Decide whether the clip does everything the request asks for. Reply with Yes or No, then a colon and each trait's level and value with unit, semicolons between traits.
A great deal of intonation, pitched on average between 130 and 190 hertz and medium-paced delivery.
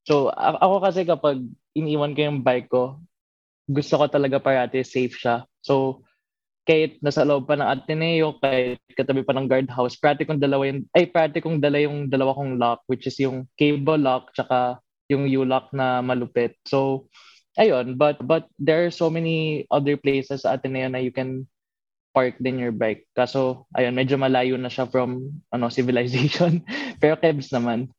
No: average, 2.8 semitones; low, 135 Hz; average, 170 wpm